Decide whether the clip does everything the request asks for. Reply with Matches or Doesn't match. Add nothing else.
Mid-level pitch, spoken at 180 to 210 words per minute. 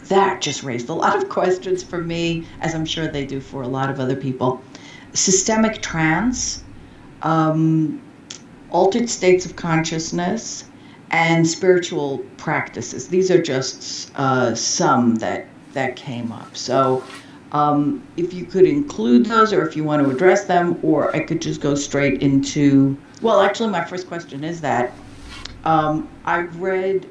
Doesn't match